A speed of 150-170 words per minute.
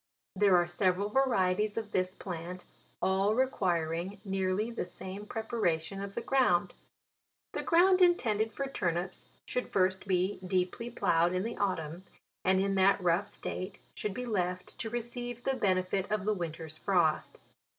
Yes: average, 155 wpm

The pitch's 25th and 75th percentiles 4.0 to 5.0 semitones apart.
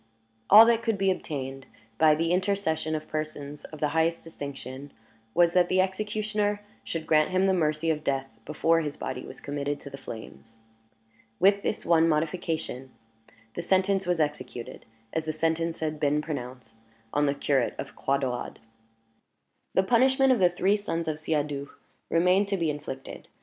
Yes: average, 4.5 semitones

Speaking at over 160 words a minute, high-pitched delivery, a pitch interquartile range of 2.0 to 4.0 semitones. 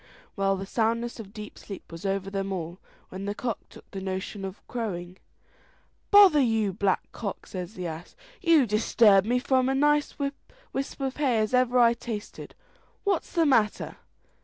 No: average, 175 wpm; high, 215 Hz; average, 4.7 semitones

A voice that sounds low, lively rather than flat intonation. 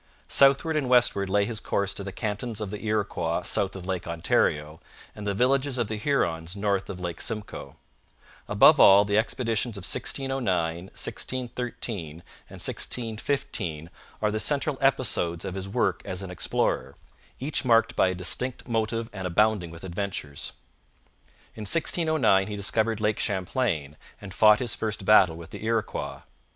No: low, 105 Hz; average, 4.1 semitones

